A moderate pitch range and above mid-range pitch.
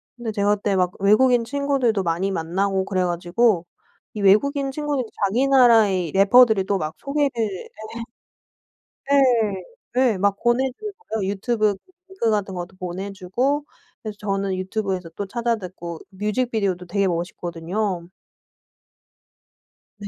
Yes: average, 4.2 semitones; high, 205 Hz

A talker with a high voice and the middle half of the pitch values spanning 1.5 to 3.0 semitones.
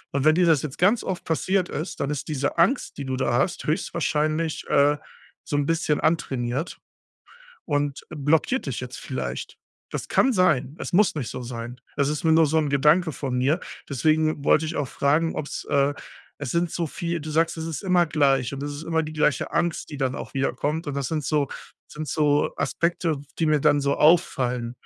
No: medium, 150 Hz; average, 2.7 semitones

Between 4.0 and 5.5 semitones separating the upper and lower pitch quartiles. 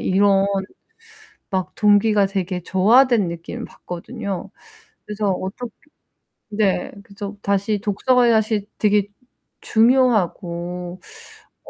No: narrow, 2.6 semitones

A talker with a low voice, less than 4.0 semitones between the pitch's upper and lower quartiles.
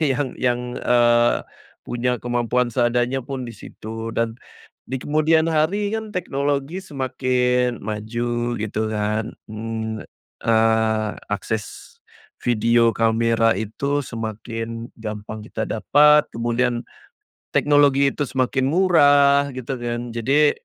Yes: low, 120 Hz; average, 3.5 semitones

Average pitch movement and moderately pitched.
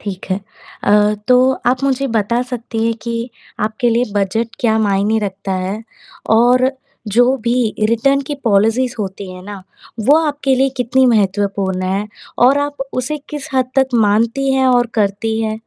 No: average, 3.8 semitones; high, 230 Hz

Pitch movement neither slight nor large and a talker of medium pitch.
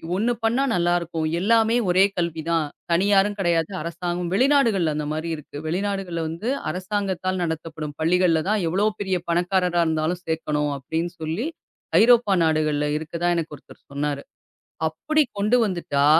Yes: average, 3.7 semitones; medium, 175 Hz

